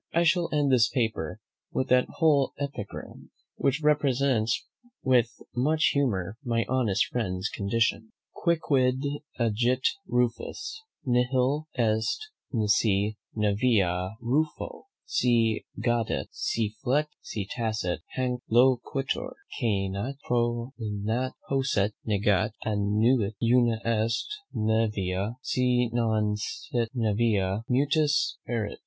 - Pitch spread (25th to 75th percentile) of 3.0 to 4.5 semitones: Yes, average, 3.4 semitones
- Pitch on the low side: Yes, low, 120 Hz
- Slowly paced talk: Yes, slow, 100 wpm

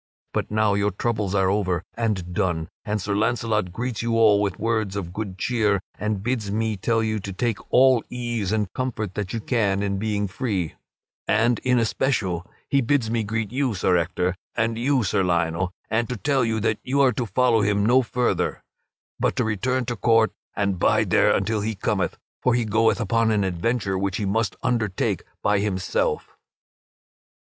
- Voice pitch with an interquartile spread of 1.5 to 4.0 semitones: Yes, average, 3.0 semitones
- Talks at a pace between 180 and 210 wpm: Yes, average, 185 wpm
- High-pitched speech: No, low, 110 Hz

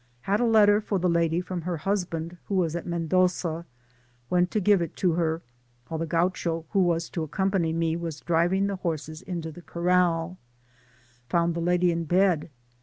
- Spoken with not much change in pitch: Yes, narrow, 1.9 semitones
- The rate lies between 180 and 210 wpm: Yes, average, 195 wpm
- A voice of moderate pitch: Yes, medium, 170 Hz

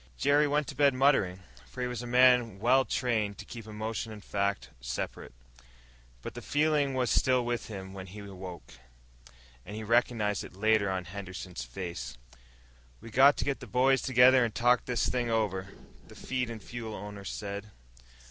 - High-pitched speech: No, low, 115 Hz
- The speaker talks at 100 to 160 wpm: No, average, 175 wpm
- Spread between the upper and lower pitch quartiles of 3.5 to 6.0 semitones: Yes, average, 4.1 semitones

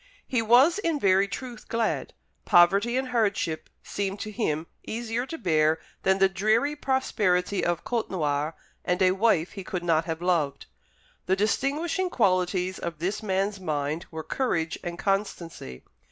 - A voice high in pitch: Yes, high, 195 Hz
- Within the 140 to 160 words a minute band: Yes, average, 150 wpm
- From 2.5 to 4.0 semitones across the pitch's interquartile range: No, average, 5.0 semitones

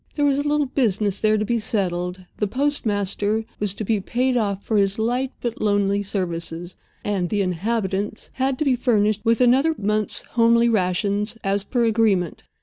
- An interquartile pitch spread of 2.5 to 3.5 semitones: Yes, average, 3.2 semitones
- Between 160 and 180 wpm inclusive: Yes, average, 170 wpm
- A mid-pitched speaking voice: No, high, 215 Hz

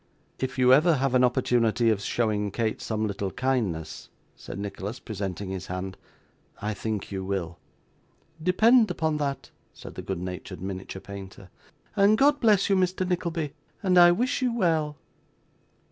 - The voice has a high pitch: No, low, 120 Hz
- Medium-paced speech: Yes, average, 155 wpm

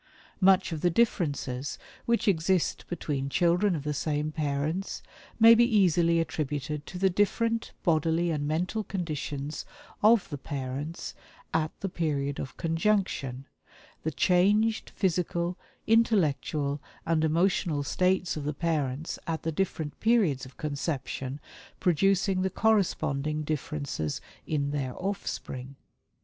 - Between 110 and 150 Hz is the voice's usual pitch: No, medium, 160 Hz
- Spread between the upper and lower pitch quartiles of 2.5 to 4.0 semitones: No, average, 4.6 semitones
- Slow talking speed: Yes, slow, 125 wpm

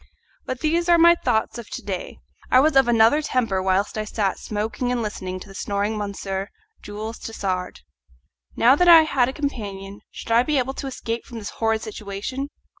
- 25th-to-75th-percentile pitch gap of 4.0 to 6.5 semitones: Yes, average, 4.7 semitones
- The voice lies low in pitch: No, high, 225 Hz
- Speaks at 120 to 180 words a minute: No, average, 195 wpm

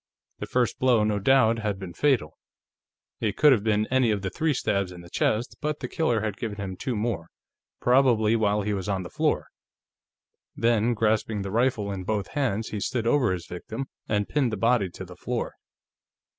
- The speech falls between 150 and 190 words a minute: No, average, 200 wpm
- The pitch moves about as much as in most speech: Yes, average, 3.4 semitones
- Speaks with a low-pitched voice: Yes, low, 110 Hz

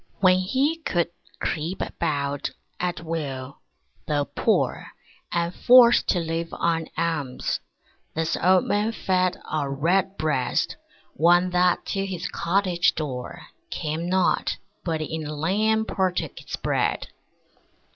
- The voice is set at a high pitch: No, medium, 170 Hz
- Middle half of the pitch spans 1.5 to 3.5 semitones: Yes, average, 3.1 semitones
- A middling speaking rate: No, slow, 120 wpm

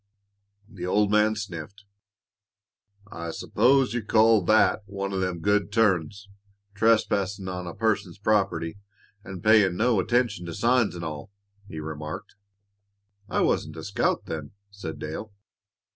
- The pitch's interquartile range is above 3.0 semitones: Yes, average, 3.8 semitones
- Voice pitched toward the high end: No, low, 100 Hz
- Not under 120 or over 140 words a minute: Yes, slow, 135 wpm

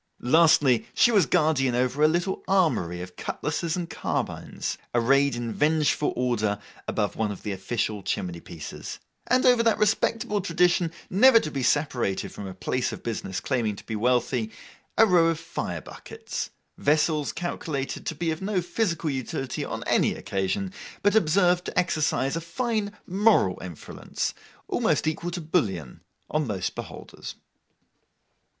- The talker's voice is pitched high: No, medium, 150 Hz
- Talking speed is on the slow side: No, average, 145 wpm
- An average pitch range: No, wide, 7.6 semitones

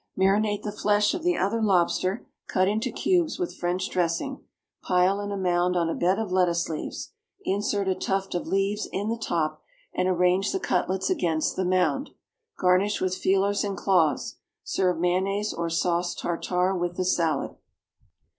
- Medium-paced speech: Yes, average, 165 wpm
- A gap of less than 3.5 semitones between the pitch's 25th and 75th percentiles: Yes, narrow, 2.4 semitones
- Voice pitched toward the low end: No, medium, 185 Hz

